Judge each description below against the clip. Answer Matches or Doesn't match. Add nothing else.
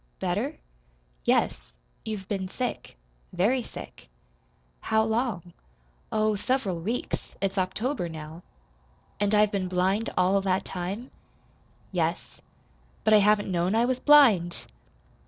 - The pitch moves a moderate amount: Matches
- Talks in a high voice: Matches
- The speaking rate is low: Matches